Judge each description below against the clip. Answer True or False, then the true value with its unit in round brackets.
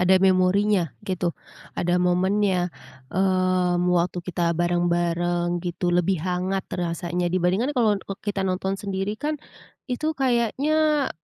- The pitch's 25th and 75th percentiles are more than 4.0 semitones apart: False (2.6 semitones)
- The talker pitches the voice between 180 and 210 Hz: True (185 Hz)